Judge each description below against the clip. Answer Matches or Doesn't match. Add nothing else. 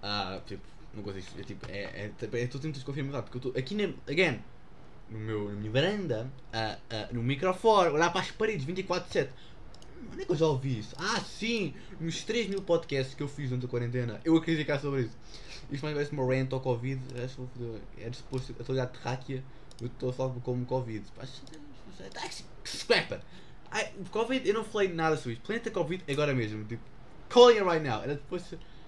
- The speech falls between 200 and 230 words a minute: Matches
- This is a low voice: Matches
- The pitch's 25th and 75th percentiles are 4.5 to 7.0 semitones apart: Matches